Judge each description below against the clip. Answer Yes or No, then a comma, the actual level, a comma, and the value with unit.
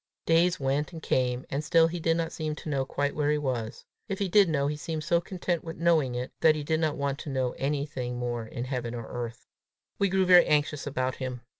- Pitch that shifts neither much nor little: Yes, average, 4.2 semitones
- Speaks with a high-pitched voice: No, medium, 150 Hz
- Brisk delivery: Yes, fast, 240 wpm